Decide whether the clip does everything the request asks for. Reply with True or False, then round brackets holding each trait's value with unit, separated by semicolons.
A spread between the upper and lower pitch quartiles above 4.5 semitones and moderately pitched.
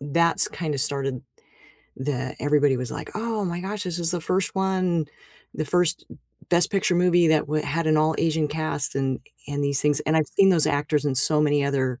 False (3.5 semitones; 155 Hz)